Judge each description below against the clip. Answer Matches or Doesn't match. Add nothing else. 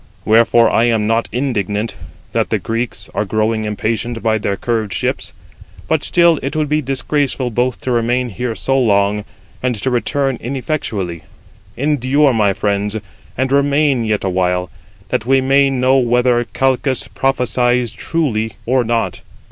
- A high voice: Doesn't match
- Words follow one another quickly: Doesn't match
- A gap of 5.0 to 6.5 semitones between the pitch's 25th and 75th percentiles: Doesn't match